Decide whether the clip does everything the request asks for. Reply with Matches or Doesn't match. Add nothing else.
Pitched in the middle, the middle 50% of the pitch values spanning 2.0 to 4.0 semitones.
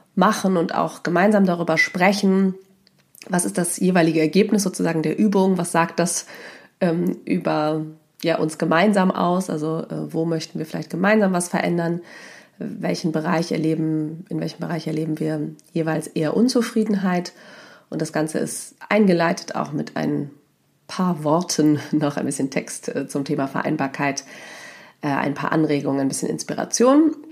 Matches